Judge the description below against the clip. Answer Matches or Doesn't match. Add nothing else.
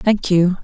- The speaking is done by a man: Doesn't match